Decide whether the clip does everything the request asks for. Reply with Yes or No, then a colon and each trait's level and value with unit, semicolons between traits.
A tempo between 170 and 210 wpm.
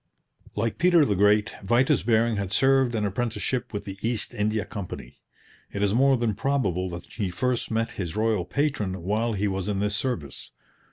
Yes: average, 180 wpm